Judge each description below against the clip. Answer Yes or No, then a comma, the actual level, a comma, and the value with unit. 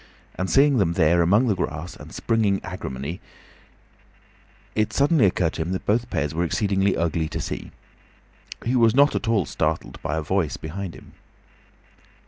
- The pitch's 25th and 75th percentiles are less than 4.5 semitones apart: No, average, 5.3 semitones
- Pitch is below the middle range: Yes, very low, 95 Hz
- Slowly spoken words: No, average, 165 wpm